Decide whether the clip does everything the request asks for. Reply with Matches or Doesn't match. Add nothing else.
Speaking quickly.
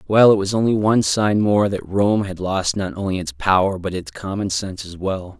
Matches